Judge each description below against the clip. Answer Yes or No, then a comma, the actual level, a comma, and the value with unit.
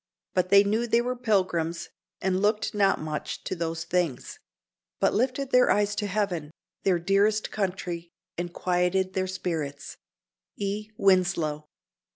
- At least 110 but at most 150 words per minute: Yes, average, 140 wpm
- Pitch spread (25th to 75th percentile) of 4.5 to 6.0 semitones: No, average, 3.3 semitones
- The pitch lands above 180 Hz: Yes, high, 190 Hz